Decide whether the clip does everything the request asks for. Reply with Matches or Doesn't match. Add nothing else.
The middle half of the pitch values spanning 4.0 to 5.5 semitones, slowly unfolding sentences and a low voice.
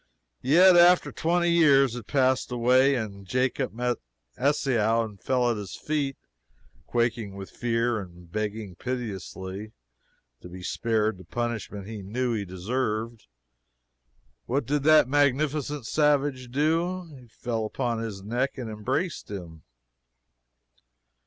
Matches